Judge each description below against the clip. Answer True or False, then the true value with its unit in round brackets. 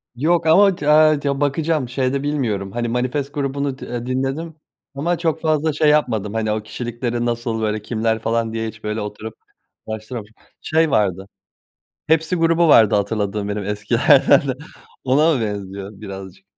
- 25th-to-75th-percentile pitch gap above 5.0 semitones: True (5.6 semitones)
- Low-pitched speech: True (120 Hz)